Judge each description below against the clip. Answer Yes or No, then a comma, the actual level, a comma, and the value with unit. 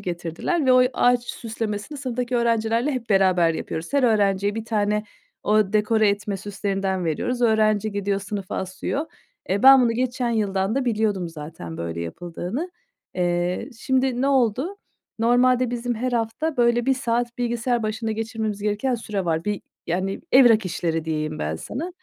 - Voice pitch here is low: No, high, 220 Hz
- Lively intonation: No, average, 4.2 semitones